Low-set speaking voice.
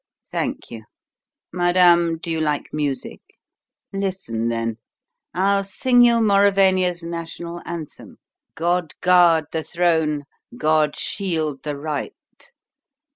No: medium, 170 Hz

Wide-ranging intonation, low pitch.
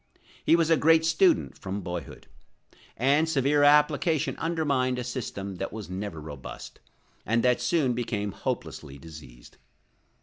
Yes: wide, 7.7 semitones; low, 125 Hz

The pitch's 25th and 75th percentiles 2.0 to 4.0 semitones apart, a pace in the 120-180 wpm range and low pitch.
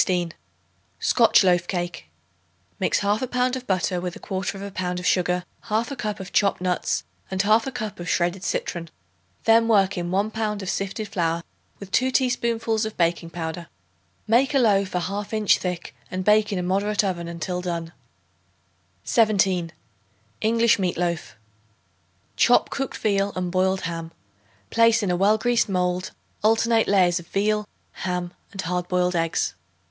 No: average, 3.3 semitones; average, 155 wpm; high, 195 Hz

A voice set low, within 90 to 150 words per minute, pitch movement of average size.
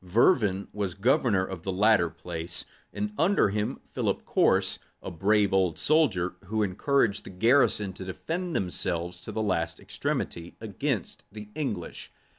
Yes: low, 100 Hz; average, 145 wpm; average, 3.8 semitones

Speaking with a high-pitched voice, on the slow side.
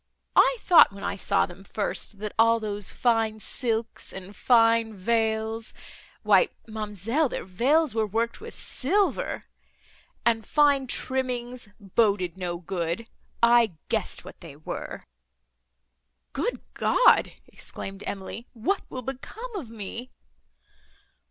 Yes: high, 225 Hz; slow, 115 wpm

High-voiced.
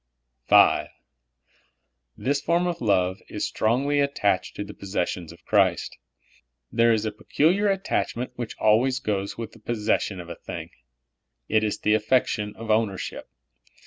No: low, 110 Hz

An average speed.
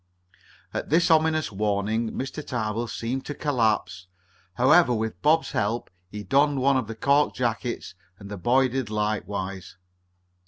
Yes: average, 145 wpm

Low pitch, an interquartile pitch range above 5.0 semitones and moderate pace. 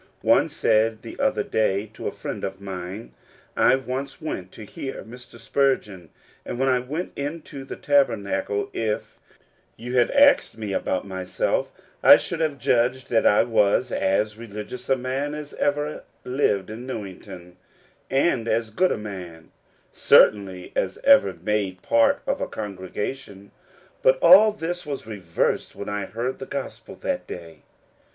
Yes: low, 115 Hz; wide, 5.4 semitones; average, 155 wpm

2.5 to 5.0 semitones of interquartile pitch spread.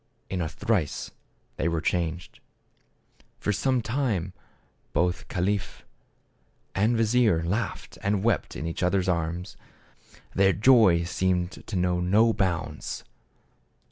Yes: average, 3.6 semitones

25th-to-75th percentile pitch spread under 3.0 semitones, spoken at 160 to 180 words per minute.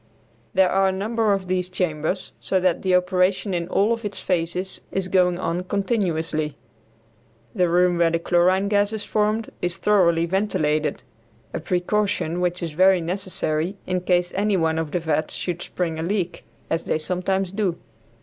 Yes: narrow, 2.4 semitones; average, 170 wpm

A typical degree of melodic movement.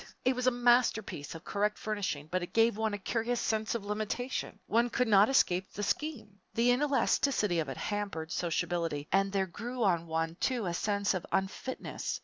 Yes: average, 5.0 semitones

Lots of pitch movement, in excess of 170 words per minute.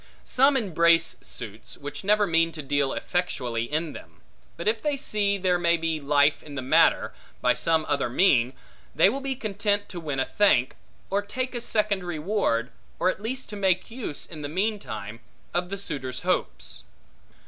Yes: wide, 6.2 semitones; average, 180 wpm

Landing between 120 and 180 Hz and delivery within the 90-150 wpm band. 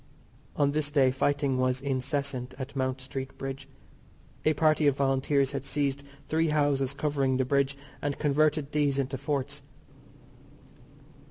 Yes: medium, 140 Hz; average, 140 wpm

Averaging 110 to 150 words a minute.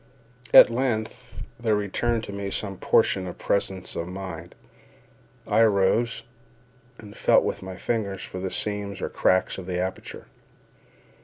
Yes: average, 145 wpm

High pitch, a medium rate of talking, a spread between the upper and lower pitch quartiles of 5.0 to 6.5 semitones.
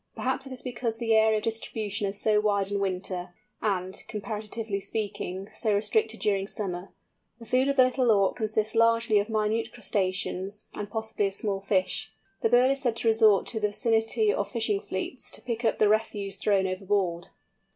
No: high, 215 Hz; average, 185 wpm; narrow, 2.4 semitones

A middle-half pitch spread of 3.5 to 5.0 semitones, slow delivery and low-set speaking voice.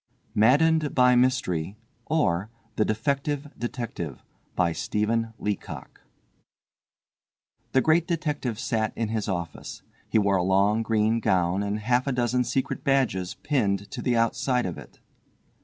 Yes: average, 4.3 semitones; slow, 125 wpm; low, 115 Hz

